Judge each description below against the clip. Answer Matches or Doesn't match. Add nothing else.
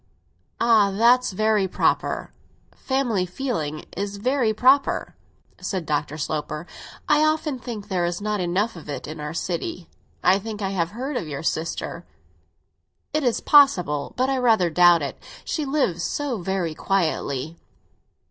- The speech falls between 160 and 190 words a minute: Doesn't match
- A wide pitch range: Matches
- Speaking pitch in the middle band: Doesn't match